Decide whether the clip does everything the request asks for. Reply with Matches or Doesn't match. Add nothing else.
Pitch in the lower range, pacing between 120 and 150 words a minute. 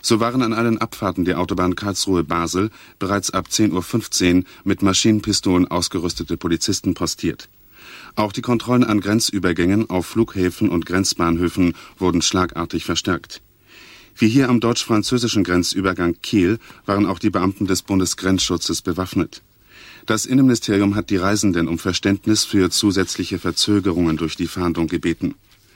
Matches